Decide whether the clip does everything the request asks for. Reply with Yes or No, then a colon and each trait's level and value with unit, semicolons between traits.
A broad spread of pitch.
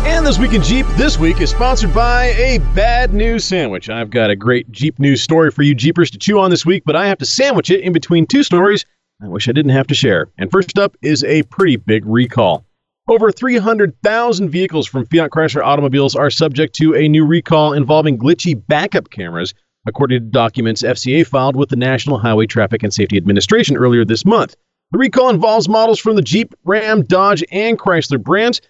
Yes: wide, 7.6 semitones